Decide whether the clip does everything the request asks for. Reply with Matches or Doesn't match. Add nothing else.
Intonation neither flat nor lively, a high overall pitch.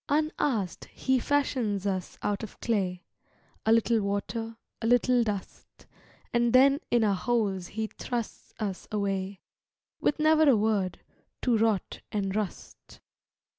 Matches